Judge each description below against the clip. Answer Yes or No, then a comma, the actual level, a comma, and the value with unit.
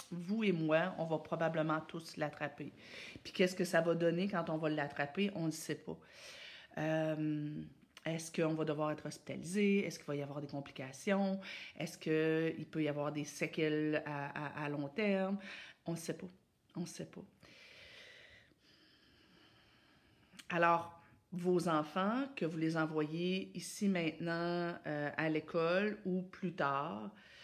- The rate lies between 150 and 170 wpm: Yes, average, 155 wpm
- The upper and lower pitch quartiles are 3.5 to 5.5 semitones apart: No, average, 3.0 semitones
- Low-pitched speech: No, medium, 165 Hz